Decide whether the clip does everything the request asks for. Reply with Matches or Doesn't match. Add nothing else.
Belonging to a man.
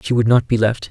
Matches